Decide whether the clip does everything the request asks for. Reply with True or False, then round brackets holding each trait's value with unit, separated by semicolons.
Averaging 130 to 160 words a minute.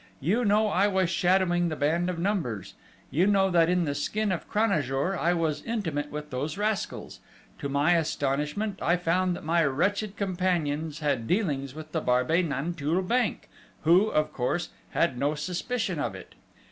False (170 wpm)